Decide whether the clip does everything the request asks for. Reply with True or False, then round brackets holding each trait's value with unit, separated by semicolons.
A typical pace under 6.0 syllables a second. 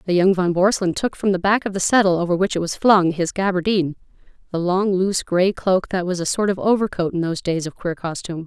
False (6.2 syllables/s)